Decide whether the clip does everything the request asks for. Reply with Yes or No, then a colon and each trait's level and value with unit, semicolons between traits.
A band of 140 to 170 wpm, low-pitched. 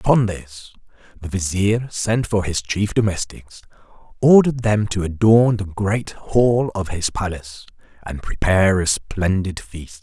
Yes: average, 145 wpm; low, 100 Hz